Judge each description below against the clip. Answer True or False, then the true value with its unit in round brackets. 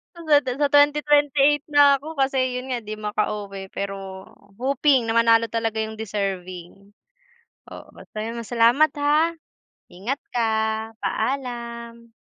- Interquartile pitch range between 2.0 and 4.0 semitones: False (4.8 semitones)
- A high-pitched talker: True (235 Hz)